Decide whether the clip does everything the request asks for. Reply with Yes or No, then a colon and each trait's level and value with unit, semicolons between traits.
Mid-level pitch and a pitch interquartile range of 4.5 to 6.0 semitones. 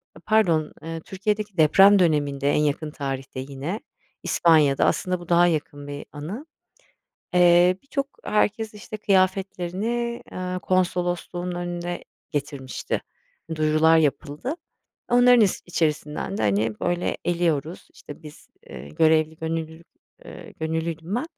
No: medium, 170 Hz; average, 3.8 semitones